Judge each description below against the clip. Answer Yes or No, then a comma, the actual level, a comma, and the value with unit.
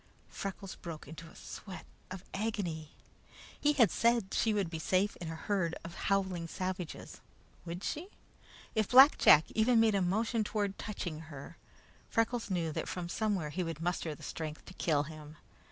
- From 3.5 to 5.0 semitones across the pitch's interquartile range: Yes, average, 4.5 semitones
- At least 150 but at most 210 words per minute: Yes, average, 170 wpm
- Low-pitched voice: No, medium, 185 Hz